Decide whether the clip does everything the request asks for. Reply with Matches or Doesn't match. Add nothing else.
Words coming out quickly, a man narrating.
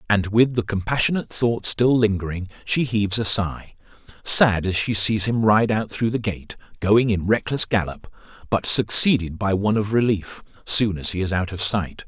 Doesn't match